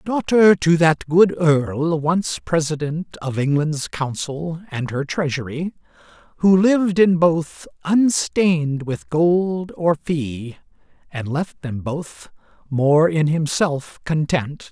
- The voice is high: No, medium, 160 Hz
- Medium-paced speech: No, slow, 120 wpm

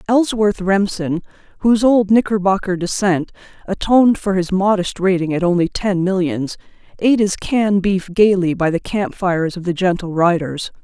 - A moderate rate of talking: Yes, average, 150 wpm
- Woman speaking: Yes, female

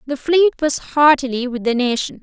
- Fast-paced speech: No, average, 190 wpm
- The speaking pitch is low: No, very high, 275 Hz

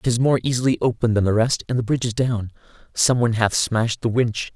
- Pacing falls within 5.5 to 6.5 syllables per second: Yes, 6.2 syllables/s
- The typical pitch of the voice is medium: No, low, 115 Hz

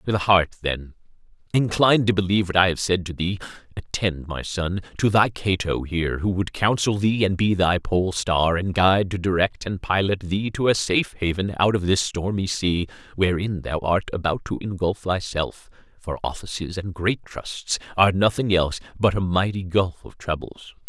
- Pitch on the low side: Yes, very low, 95 Hz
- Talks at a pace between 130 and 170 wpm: No, average, 185 wpm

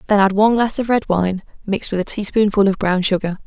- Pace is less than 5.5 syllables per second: No, 6.3 syllables/s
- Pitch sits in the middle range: No, high, 200 Hz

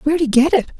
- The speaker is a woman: No, male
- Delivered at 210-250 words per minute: No, fast, 305 wpm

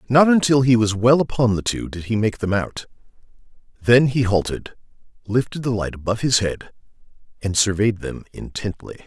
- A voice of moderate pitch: No, low, 115 Hz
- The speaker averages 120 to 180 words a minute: Yes, average, 170 wpm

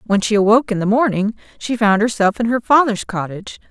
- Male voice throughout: No, female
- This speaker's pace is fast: Yes, fast, 210 wpm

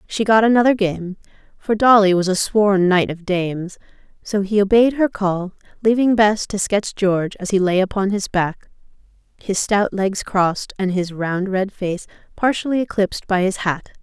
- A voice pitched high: Yes, high, 200 Hz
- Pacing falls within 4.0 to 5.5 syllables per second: Yes, 4.8 syllables/s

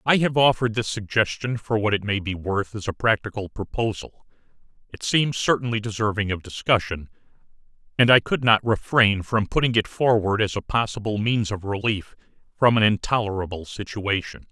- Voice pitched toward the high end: No, low, 110 Hz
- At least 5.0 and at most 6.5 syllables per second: Yes, 5.3 syllables/s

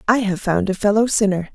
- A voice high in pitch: Yes, high, 205 Hz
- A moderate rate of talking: No, fast, 235 wpm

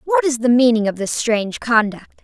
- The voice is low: No, high, 235 Hz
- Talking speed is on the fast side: Yes, fast, 215 wpm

